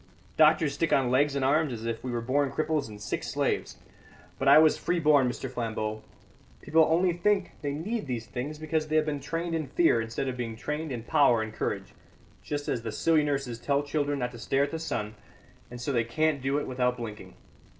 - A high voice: No, medium, 140 Hz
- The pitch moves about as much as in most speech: Yes, average, 4.3 semitones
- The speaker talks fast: Yes, fast, 220 wpm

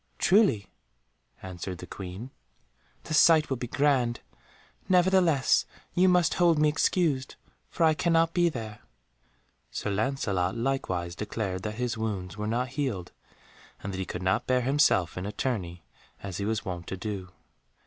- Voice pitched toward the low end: Yes, low, 115 Hz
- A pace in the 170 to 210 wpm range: No, average, 155 wpm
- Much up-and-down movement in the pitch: Yes, wide, 8.0 semitones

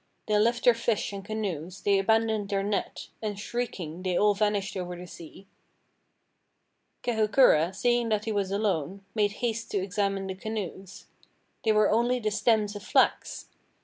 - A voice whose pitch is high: Yes, high, 205 Hz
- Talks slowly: No, average, 160 wpm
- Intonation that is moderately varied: No, narrow, 2.3 semitones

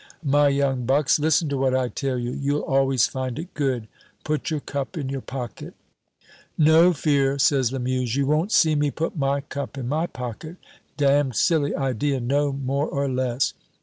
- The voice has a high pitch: No, medium, 140 Hz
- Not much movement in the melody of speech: Yes, narrow, 2.0 semitones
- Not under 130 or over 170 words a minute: No, average, 180 wpm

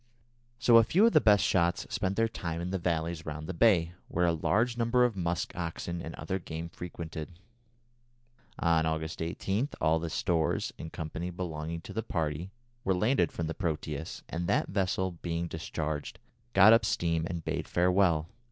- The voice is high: No, very low, 85 Hz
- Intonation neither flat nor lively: Yes, average, 3.0 semitones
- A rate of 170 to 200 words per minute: Yes, average, 175 wpm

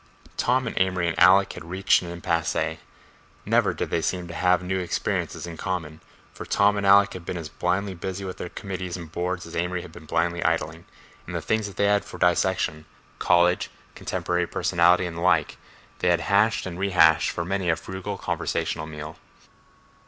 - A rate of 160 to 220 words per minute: Yes, average, 180 wpm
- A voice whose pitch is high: No, very low, 90 Hz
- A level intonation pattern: Yes, narrow, 2.0 semitones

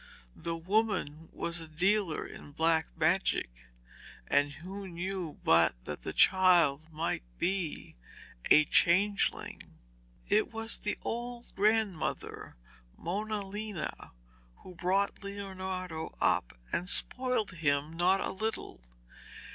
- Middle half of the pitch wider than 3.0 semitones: Yes, average, 4.0 semitones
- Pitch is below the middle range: No, medium, 185 Hz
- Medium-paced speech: No, slow, 110 wpm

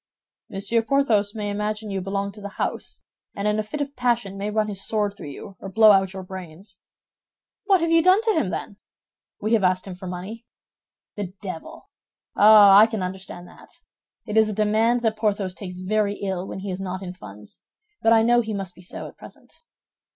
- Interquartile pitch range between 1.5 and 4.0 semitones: Yes, narrow, 2.5 semitones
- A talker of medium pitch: No, high, 205 Hz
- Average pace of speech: No, fast, 210 wpm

